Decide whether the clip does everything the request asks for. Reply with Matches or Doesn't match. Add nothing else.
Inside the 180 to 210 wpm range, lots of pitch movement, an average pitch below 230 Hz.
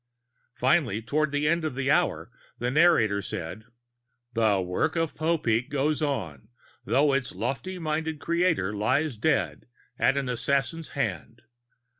Doesn't match